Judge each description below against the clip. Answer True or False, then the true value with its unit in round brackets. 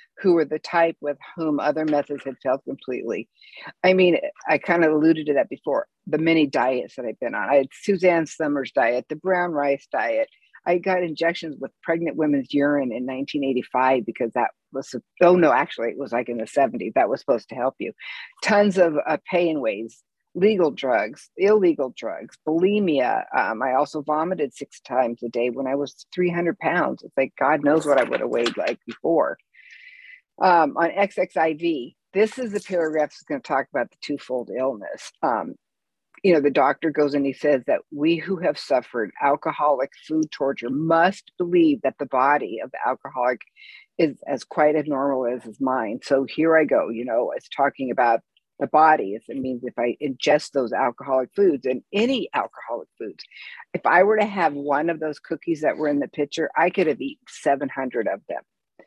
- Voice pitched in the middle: True (155 Hz)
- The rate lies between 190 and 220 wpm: True (195 wpm)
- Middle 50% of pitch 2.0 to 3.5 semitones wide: False (4.5 semitones)